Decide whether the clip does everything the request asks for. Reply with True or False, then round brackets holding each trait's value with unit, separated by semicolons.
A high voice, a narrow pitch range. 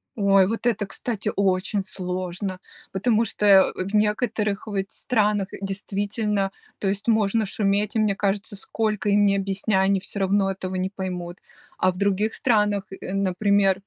True (200 Hz; 1.6 semitones)